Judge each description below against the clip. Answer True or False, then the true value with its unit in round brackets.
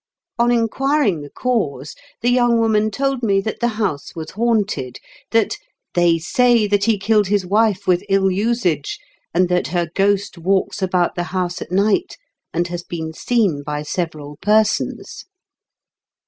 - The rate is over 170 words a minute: False (160 wpm)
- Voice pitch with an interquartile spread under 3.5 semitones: False (4.5 semitones)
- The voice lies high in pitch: True (195 Hz)